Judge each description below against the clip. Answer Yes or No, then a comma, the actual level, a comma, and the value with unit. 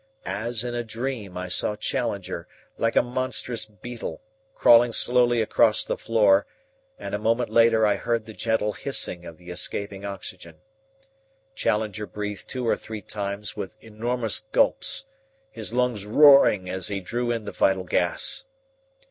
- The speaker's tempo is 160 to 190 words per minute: No, average, 150 wpm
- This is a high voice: No, low, 110 Hz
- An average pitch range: Yes, average, 3.2 semitones